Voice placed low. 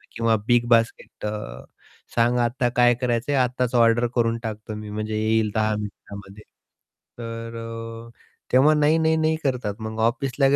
Yes: low, 115 Hz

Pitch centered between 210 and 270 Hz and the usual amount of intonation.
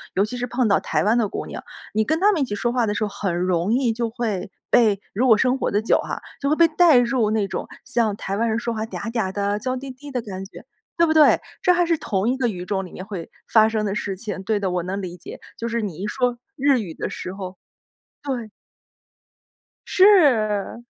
Yes: high, 220 Hz; average, 4.2 semitones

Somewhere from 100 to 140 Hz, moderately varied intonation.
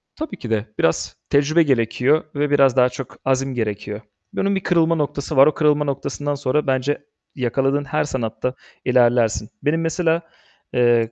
Yes: low, 135 Hz; average, 3.4 semitones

